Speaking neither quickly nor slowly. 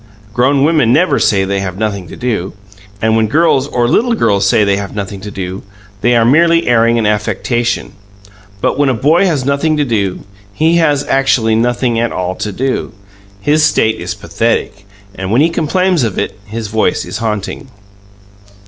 Yes: average, 185 wpm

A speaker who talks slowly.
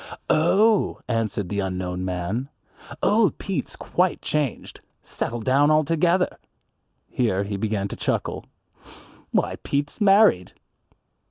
Yes: slow, 105 wpm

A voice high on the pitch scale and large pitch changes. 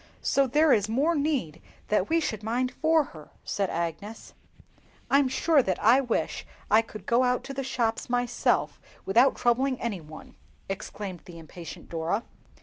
Yes: high, 235 Hz; wide, 5.7 semitones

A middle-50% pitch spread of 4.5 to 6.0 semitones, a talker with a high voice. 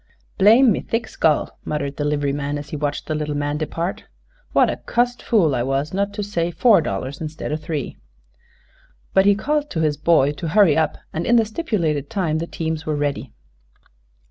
No: wide, 5.4 semitones; medium, 155 Hz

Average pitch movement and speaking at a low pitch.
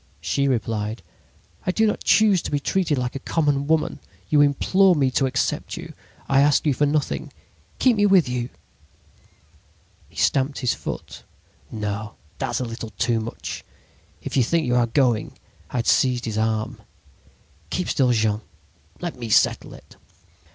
Yes: average, 4.7 semitones; low, 130 Hz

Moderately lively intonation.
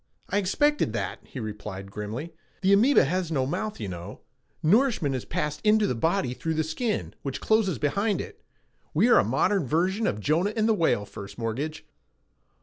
No: wide, 8.7 semitones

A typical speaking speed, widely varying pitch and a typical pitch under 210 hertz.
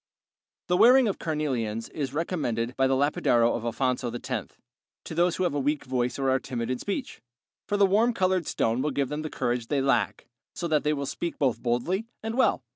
No: fast, 210 wpm; wide, 6.0 semitones; medium, 140 Hz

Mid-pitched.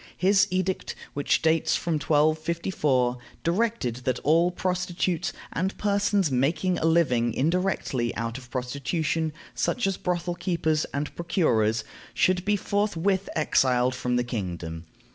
Yes: medium, 160 Hz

